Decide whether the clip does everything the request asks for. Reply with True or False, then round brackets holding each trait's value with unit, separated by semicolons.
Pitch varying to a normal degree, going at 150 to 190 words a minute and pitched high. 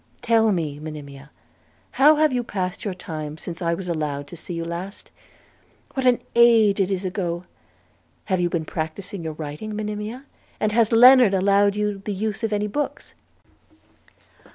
True (4.4 semitones; 160 wpm; 195 Hz)